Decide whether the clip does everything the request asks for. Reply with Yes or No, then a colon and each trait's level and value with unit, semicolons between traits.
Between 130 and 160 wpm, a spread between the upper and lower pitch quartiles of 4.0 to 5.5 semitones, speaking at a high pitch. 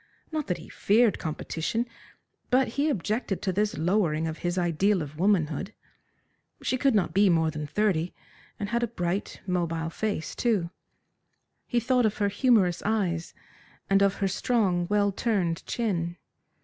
Yes: average, 155 wpm; average, 4.3 semitones; high, 195 Hz